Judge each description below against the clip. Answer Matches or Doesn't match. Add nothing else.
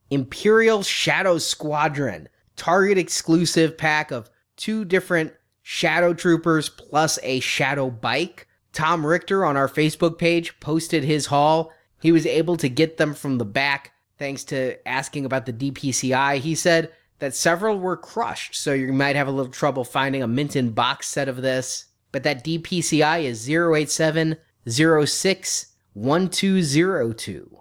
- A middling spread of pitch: Matches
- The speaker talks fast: Doesn't match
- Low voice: Doesn't match